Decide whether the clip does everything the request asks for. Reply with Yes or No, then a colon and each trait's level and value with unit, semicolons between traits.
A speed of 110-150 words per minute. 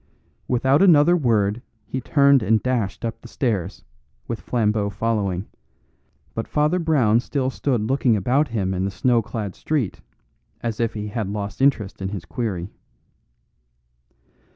Yes: average, 145 wpm